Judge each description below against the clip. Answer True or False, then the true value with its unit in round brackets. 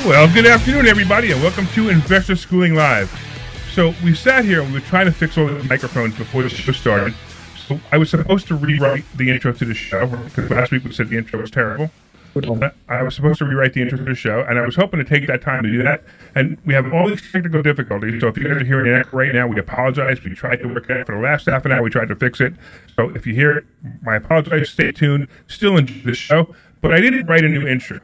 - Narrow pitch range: False (4.5 semitones)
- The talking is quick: True (265 wpm)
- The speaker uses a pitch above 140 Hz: False (135 Hz)